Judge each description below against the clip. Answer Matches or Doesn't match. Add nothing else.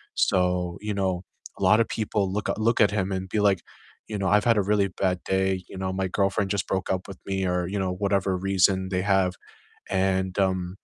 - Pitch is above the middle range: Doesn't match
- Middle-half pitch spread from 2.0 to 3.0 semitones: Doesn't match